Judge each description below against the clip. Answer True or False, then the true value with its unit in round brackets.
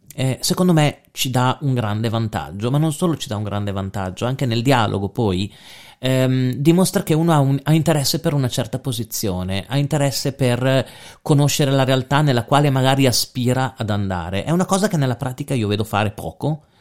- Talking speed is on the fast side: True (195 wpm)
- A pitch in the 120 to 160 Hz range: True (130 Hz)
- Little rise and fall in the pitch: False (4.2 semitones)